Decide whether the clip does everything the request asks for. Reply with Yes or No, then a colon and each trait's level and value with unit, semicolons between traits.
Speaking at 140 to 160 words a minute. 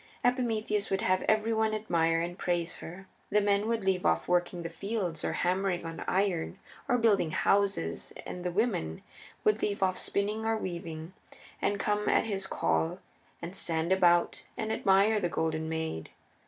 No: average, 170 wpm